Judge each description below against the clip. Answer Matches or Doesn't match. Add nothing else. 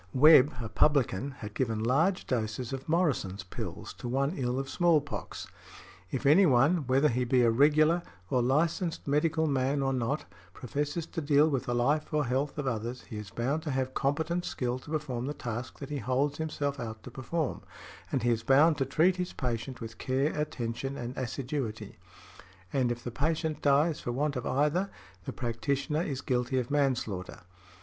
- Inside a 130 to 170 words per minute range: Doesn't match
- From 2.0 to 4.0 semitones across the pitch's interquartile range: Matches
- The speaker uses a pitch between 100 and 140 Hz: Matches